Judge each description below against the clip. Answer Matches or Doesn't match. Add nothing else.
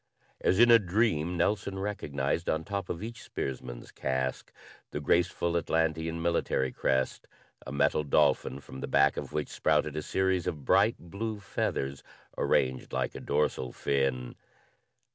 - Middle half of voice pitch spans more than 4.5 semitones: Matches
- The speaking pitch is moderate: Doesn't match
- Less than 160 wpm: Matches